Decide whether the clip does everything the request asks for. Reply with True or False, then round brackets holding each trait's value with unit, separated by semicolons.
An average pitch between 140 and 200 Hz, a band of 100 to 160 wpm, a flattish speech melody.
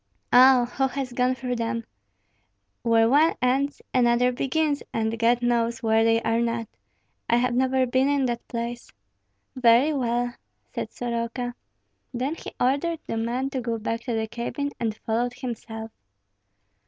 False (245 Hz; 155 wpm; 1.9 semitones)